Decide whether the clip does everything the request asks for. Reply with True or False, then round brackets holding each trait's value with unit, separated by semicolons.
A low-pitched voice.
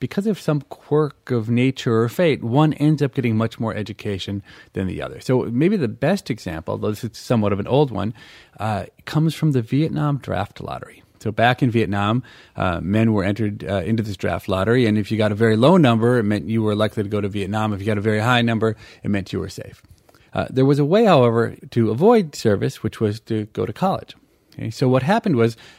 True (115 Hz)